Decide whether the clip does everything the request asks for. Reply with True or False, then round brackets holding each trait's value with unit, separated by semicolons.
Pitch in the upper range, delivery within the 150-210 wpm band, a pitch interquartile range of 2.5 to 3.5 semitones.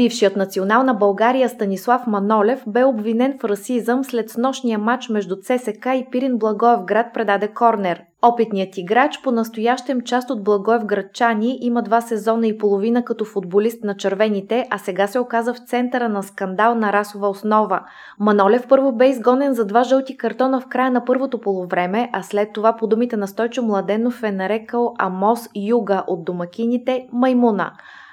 True (230 Hz; 160 wpm; 3.1 semitones)